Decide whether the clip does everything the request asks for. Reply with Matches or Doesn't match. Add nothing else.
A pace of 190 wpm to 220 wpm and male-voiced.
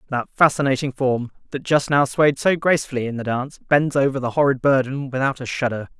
Matches